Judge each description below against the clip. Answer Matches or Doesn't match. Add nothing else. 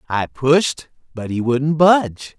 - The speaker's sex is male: Matches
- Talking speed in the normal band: Matches